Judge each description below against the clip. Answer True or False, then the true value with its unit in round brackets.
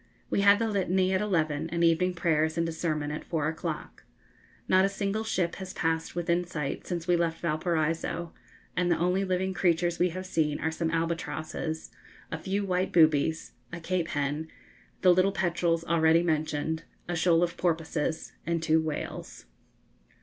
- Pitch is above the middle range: False (170 Hz)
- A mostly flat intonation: True (2.1 semitones)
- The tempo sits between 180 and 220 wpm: False (170 wpm)